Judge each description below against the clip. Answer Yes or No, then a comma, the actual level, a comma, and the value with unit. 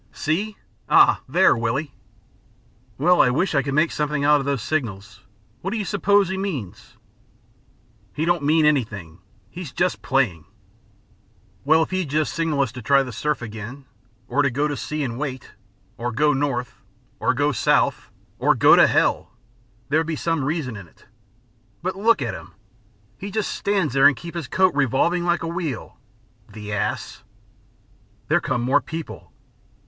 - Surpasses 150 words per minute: Yes, average, 170 wpm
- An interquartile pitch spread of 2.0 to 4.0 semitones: No, average, 5.1 semitones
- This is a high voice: No, medium, 145 Hz